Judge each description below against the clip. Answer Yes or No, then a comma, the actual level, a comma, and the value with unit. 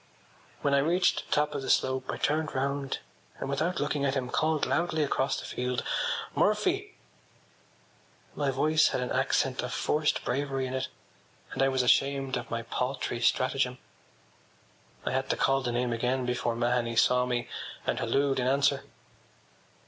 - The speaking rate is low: No, average, 165 wpm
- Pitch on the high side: No, low, 135 Hz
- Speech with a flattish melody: Yes, narrow, 2.3 semitones